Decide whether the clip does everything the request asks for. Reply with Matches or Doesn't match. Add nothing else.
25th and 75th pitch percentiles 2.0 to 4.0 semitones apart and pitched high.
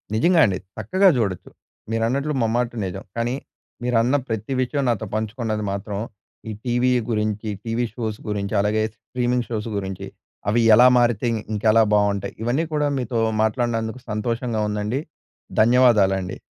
Doesn't match